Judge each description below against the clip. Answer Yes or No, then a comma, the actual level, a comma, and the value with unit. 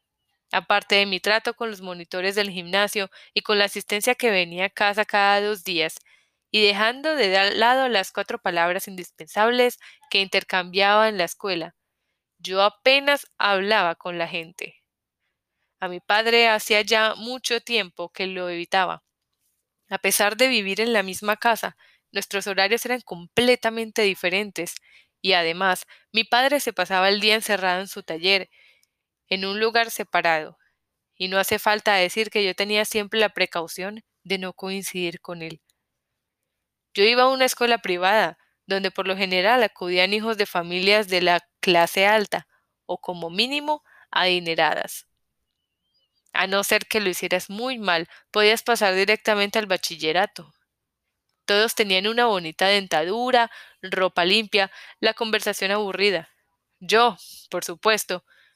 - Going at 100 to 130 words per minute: No, average, 145 wpm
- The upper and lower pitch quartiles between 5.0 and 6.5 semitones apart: No, average, 3.1 semitones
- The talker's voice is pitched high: Yes, high, 200 Hz